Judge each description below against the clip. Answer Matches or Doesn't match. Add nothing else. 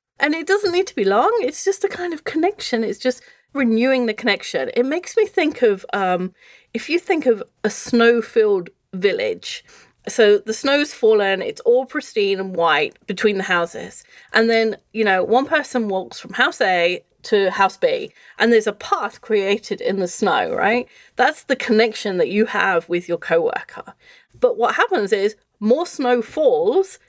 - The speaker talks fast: Doesn't match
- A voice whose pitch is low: Doesn't match